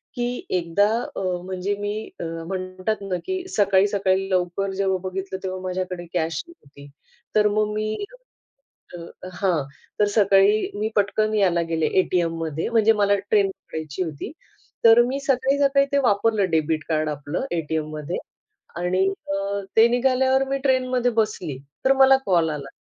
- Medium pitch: No, high, 195 Hz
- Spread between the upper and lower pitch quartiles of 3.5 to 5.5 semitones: Yes, average, 4.1 semitones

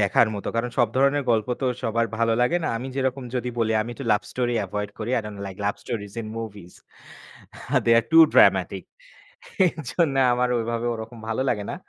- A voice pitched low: Yes, low, 115 Hz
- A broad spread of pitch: No, average, 2.7 semitones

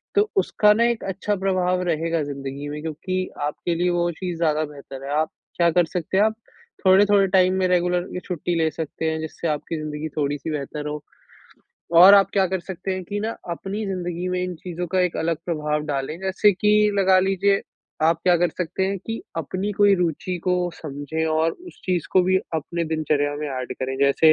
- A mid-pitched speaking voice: Yes, medium, 175 Hz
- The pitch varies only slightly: No, average, 3.4 semitones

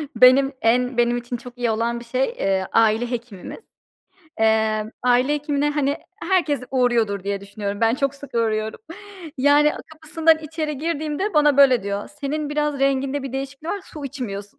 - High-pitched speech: Yes, very high, 260 Hz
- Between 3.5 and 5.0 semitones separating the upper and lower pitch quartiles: Yes, average, 4.5 semitones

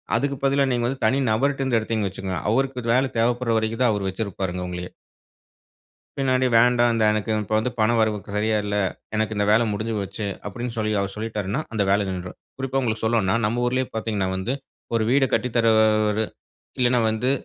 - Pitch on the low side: Yes, low, 110 Hz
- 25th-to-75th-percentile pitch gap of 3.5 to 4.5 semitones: No, average, 2.9 semitones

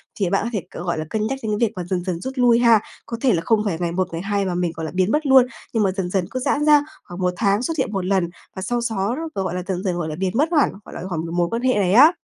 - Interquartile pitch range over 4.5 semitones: Yes, average, 4.9 semitones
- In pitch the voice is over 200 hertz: No, high, 195 Hz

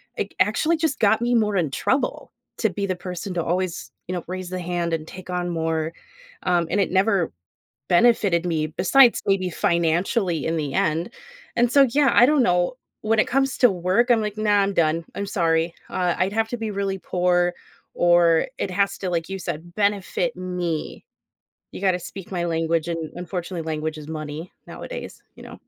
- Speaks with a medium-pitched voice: Yes, medium, 180 Hz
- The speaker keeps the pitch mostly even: No, average, 3.4 semitones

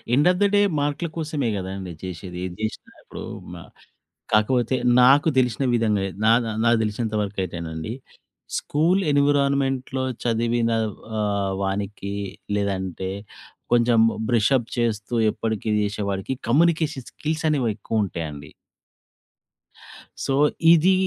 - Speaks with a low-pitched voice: Yes, low, 115 Hz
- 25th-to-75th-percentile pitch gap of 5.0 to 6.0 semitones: Yes, wide, 5.6 semitones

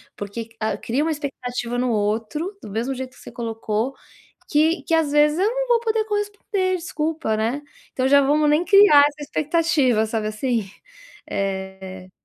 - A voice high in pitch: Yes, very high, 275 Hz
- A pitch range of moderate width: No, wide, 6.5 semitones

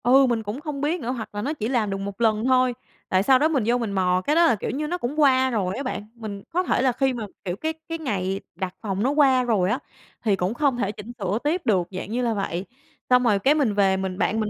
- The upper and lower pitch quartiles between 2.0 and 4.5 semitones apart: No, average, 5.1 semitones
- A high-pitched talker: Yes, high, 235 Hz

